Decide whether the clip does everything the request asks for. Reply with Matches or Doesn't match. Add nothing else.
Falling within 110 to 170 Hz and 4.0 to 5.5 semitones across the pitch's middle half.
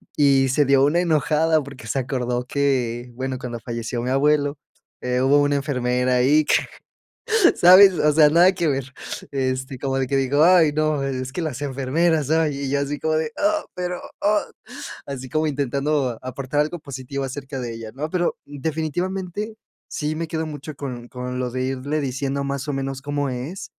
Doesn't match